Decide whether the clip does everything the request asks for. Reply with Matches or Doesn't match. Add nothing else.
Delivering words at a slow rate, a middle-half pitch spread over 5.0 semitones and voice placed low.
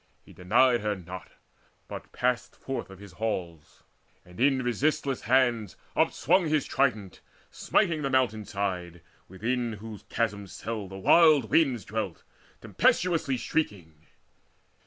Matches